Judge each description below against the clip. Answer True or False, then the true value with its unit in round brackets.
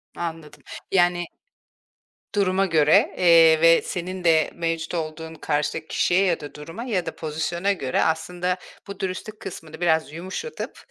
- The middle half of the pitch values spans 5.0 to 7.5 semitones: False (2.4 semitones)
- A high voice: False (170 Hz)